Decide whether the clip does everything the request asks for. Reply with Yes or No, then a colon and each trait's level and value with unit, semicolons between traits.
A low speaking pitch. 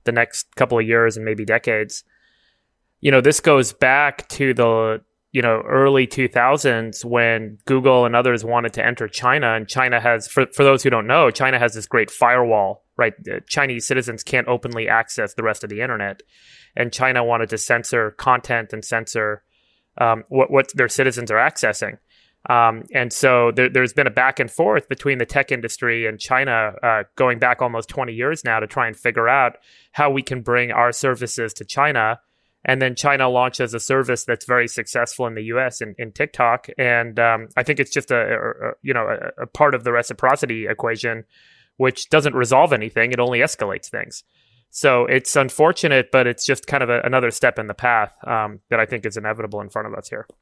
Yes: low, 120 Hz